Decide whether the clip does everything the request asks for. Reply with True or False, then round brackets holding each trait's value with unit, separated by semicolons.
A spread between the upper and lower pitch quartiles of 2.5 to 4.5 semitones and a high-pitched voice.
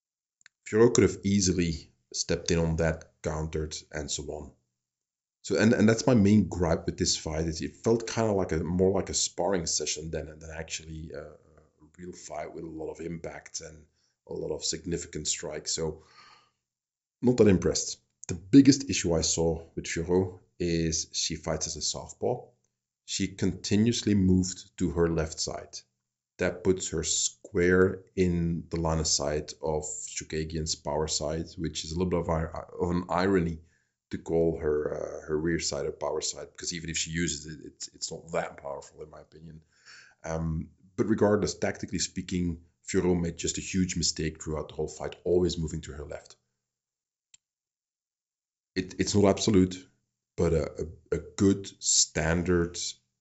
False (2.9 semitones; 85 Hz)